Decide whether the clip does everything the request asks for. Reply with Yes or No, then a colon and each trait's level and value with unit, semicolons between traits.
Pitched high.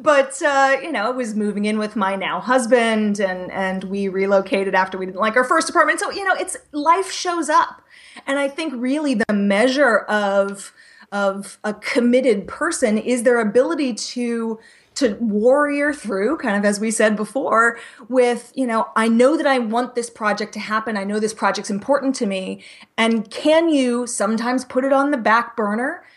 Yes: high, 235 Hz